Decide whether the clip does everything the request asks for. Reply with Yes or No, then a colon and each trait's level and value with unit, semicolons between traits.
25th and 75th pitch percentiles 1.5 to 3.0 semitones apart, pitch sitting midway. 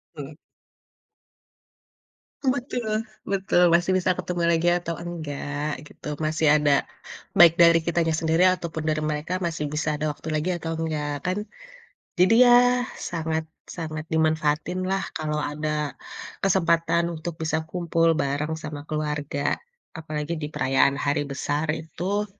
Yes: narrow, 2.4 semitones; medium, 160 Hz